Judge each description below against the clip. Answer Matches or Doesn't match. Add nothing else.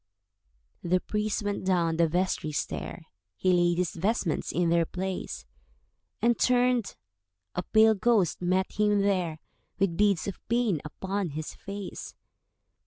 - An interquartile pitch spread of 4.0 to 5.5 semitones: Doesn't match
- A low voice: Doesn't match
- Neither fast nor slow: Doesn't match